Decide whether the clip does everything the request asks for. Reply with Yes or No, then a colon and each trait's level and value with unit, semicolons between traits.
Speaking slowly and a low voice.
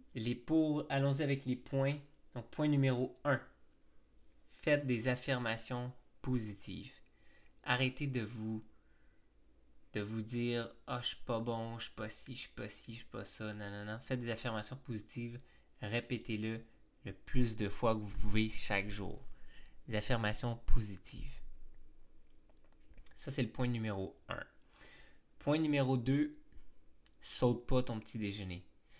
No: average, 155 wpm; low, 115 Hz